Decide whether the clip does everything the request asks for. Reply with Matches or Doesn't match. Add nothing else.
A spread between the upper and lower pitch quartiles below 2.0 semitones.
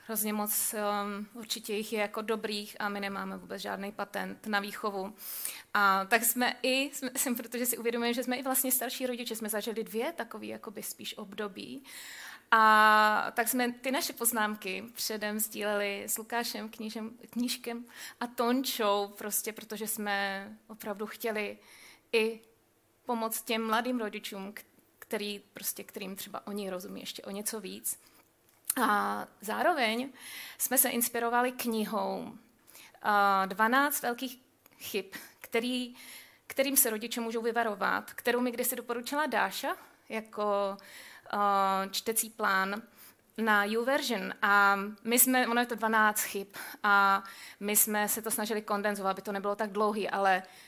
Doesn't match